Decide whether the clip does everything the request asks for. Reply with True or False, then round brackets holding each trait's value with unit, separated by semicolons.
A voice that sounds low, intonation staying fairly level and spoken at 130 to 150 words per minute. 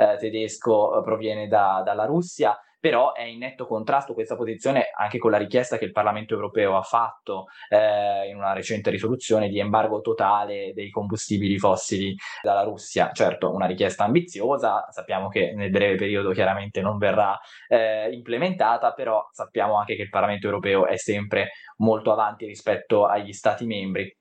False (105 Hz; 1.7 semitones; 160 wpm)